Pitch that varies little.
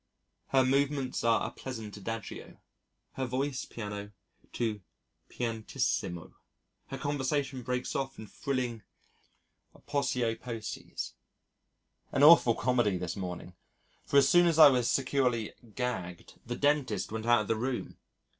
No: average, 3.7 semitones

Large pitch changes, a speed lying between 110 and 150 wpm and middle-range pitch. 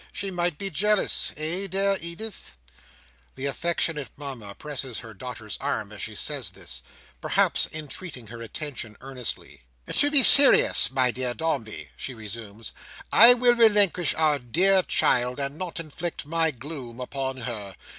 Yes: wide, 6.3 semitones; average, 145 wpm; medium, 145 Hz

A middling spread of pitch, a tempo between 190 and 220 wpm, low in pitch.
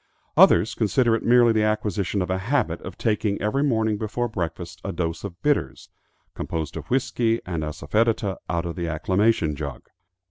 No: average, 5.0 semitones; average, 170 wpm; low, 105 Hz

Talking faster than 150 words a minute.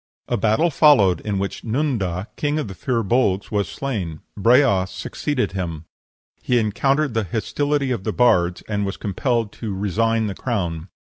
Yes: average, 160 wpm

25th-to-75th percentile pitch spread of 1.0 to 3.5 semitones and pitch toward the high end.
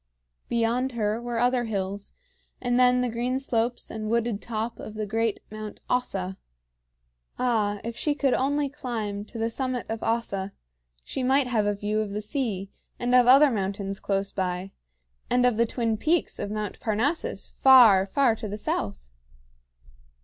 Yes: average, 3.2 semitones; high, 225 Hz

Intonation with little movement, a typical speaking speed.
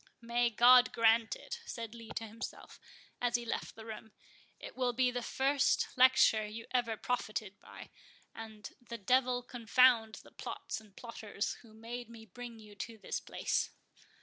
Yes: narrow, 1.9 semitones; average, 160 wpm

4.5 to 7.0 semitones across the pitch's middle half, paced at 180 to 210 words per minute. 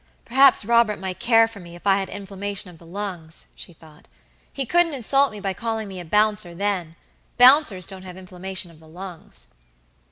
No: average, 4.1 semitones; average, 190 wpm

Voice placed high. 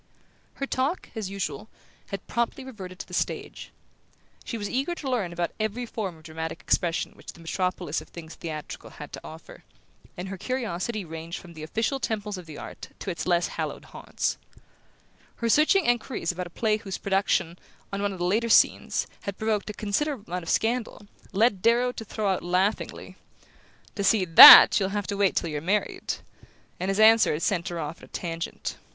Yes: high, 195 Hz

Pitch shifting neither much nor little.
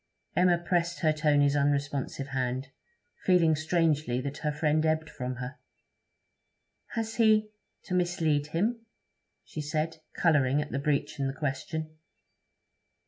Yes: average, 3.1 semitones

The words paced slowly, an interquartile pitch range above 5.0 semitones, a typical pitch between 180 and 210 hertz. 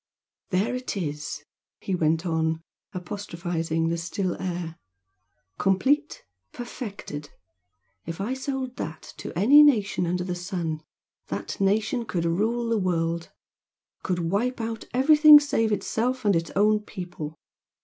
Yes: slow, 130 wpm; wide, 5.5 semitones; high, 190 Hz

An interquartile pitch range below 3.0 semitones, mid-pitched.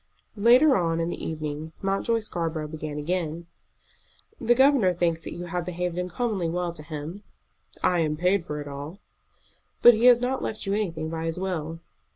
No: average, 3.7 semitones; medium, 175 Hz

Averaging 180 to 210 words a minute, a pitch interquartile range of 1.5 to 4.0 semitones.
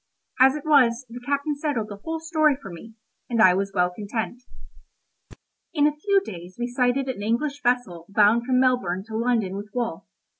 No: average, 185 wpm; wide, 5.4 semitones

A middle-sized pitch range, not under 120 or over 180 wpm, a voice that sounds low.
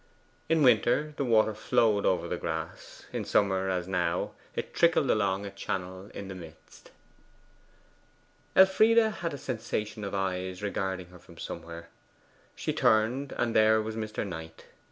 Yes: average, 4.1 semitones; average, 150 wpm; low, 100 Hz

